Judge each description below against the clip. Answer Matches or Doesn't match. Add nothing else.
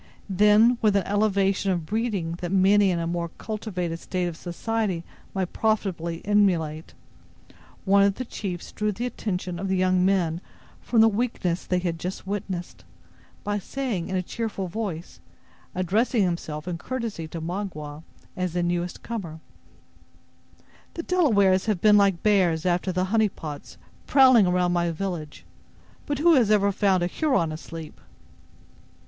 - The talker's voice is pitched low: Doesn't match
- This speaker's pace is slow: Doesn't match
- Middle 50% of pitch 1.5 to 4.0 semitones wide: Matches